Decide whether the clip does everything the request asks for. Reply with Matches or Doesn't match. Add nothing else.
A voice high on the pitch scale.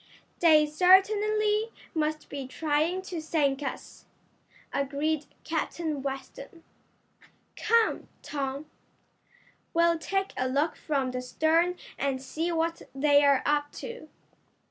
Matches